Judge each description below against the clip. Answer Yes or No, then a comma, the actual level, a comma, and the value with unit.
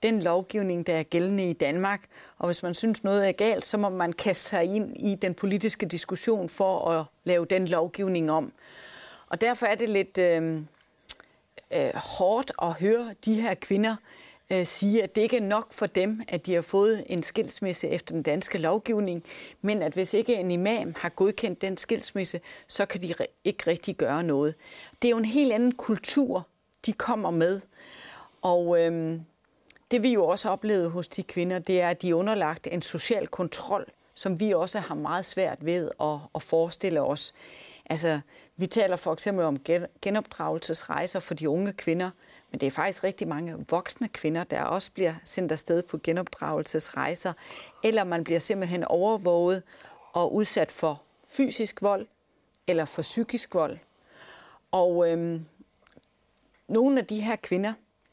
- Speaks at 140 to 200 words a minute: Yes, average, 170 wpm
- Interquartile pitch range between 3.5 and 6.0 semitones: Yes, average, 3.9 semitones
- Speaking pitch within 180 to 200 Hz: Yes, medium, 185 Hz